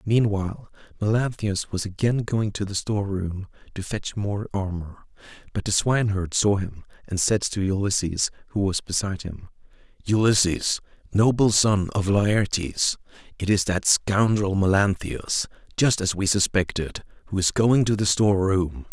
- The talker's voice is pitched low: Yes, low, 100 Hz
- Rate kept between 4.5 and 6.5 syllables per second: Yes, 4.6 syllables/s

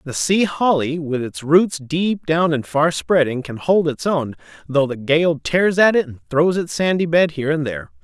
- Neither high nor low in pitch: Yes, medium, 155 Hz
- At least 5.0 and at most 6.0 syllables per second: No, 4.5 syllables/s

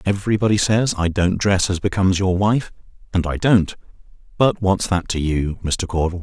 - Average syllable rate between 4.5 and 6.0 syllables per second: Yes, 5.5 syllables/s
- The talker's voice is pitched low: Yes, very low, 95 Hz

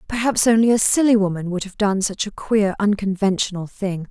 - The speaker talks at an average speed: Yes, average, 190 wpm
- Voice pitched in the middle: No, high, 200 Hz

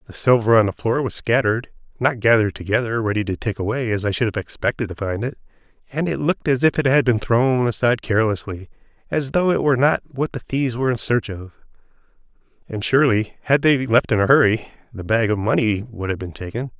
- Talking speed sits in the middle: No, fast, 220 wpm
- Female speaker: No, male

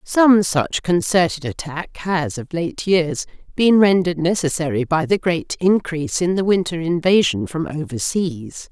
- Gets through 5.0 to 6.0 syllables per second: No, 4.4 syllables/s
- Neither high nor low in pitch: Yes, medium, 170 Hz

